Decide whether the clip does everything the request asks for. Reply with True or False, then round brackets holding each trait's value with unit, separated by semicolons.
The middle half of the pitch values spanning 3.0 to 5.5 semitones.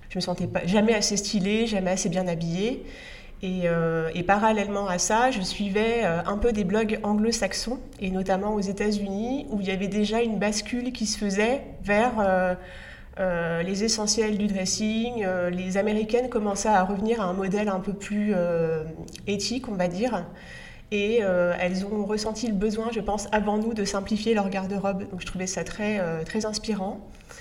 False (2.5 semitones)